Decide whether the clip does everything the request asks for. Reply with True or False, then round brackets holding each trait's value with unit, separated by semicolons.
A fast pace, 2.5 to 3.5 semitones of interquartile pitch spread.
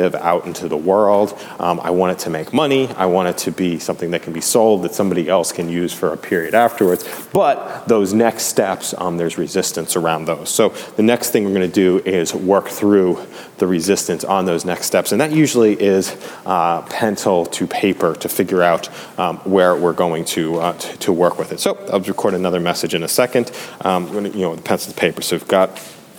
True (220 wpm; 2.8 semitones)